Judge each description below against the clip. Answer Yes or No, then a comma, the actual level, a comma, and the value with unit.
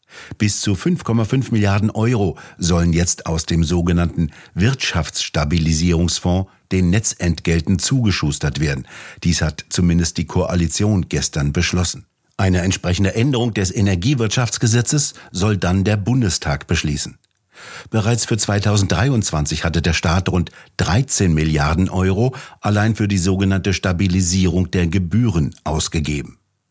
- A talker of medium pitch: No, very low, 95 Hz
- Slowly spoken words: Yes, slow, 110 wpm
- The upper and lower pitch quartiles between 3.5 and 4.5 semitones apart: Yes, average, 3.8 semitones